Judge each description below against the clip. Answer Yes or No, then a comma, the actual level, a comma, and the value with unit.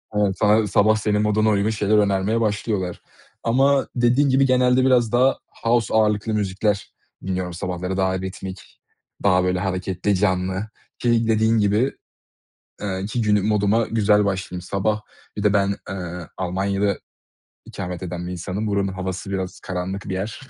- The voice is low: Yes, low, 100 Hz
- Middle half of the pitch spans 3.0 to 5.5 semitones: No, narrow, 2.6 semitones